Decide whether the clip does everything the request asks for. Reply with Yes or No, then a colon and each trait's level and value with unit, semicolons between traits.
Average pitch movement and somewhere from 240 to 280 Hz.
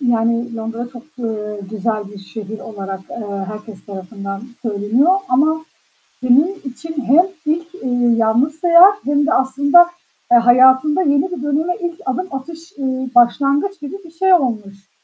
No: wide, 6.2 semitones; very high, 255 Hz